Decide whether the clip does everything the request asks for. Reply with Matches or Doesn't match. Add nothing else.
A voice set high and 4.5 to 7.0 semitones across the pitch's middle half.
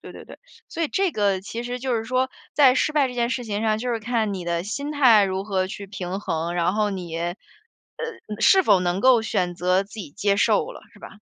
Matches